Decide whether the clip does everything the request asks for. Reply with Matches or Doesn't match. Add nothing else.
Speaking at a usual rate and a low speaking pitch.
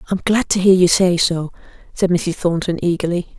Doesn't match